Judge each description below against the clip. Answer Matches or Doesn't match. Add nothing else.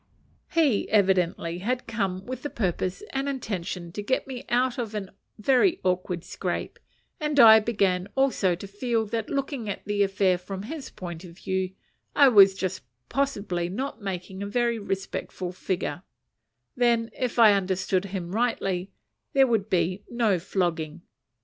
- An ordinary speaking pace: Matches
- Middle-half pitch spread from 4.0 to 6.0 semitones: Matches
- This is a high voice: Matches